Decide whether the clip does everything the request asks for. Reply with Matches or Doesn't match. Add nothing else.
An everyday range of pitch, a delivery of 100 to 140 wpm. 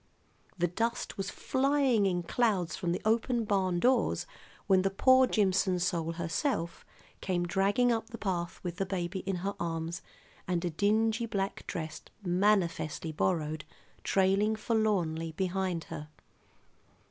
Matches